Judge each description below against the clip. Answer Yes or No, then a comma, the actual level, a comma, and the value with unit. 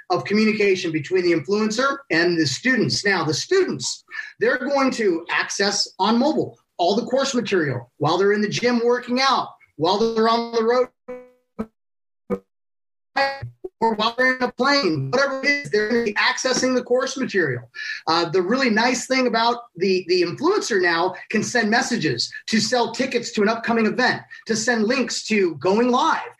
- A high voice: Yes, high, 230 Hz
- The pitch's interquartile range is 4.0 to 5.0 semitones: Yes, average, 4.7 semitones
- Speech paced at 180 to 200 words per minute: No, average, 165 wpm